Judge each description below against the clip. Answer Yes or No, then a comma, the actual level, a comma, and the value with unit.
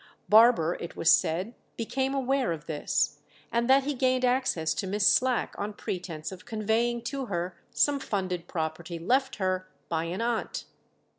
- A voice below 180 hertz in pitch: No, high, 210 Hz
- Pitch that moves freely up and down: Yes, wide, 6.6 semitones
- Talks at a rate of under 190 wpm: Yes, average, 160 wpm